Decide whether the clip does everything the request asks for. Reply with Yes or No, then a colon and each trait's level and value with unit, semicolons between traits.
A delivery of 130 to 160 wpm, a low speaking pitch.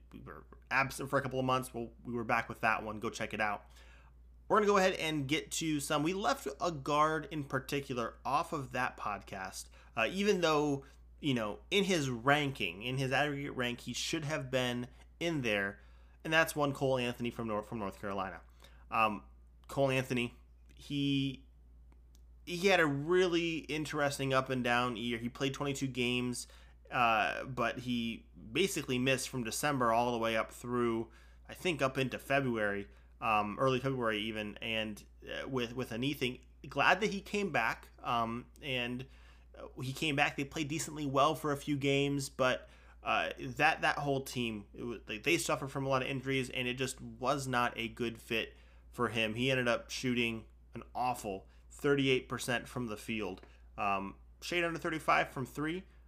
No: average, 180 wpm; low, 125 Hz